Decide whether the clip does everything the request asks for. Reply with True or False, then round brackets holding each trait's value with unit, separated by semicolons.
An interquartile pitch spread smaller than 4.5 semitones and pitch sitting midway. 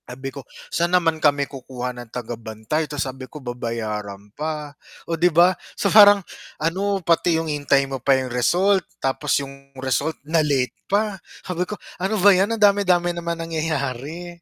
False (5.1 semitones; 155 Hz)